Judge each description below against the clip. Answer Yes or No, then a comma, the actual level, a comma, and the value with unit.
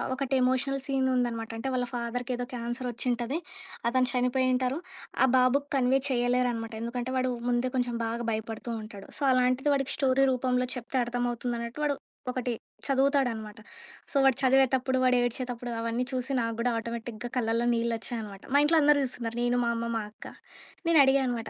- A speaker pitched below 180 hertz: No, high, 245 Hz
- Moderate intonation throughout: No, narrow, 1.8 semitones